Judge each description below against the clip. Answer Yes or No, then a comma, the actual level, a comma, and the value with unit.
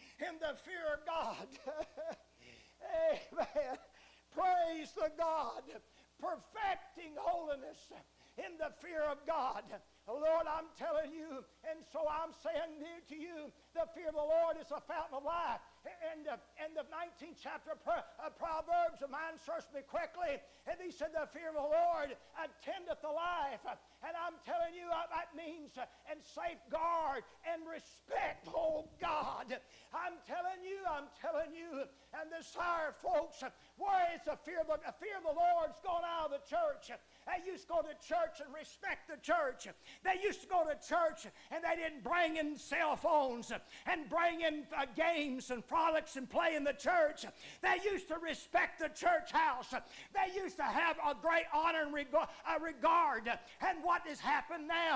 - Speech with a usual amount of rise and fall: No, narrow, 1.9 semitones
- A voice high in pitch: Yes, very high, 320 Hz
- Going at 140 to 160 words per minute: No, average, 175 wpm